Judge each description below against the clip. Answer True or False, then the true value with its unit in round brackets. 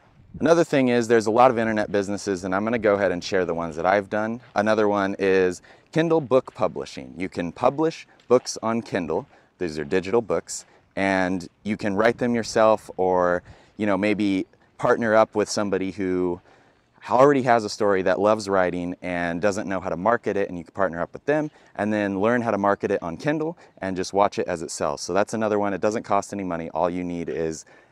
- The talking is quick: True (220 wpm)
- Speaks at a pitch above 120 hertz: False (100 Hz)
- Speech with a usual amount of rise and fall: True (3.6 semitones)